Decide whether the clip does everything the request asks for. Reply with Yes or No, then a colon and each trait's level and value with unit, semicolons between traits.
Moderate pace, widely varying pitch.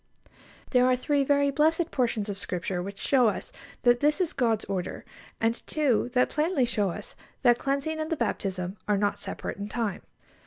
Yes: average, 185 wpm; wide, 5.7 semitones